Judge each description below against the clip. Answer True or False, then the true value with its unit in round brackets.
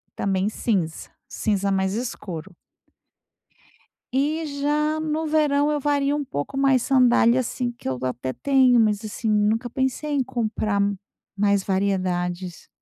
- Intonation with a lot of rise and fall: True (6.1 semitones)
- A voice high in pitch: True (235 Hz)